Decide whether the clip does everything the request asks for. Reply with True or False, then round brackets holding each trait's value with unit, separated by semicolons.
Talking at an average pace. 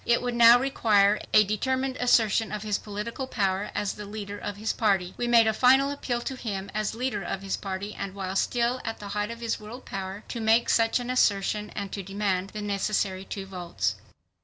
False (210 wpm)